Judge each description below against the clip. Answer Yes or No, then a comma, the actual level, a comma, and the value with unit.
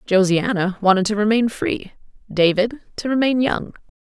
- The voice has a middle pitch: No, high, 210 Hz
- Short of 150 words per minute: Yes, slow, 135 wpm